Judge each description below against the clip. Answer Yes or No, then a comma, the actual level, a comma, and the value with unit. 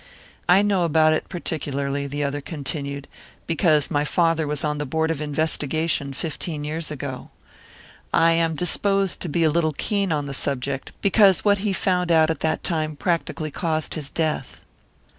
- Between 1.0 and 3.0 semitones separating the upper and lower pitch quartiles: Yes, narrow, 2.6 semitones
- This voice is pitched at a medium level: Yes, medium, 155 Hz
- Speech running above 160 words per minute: Yes, average, 170 wpm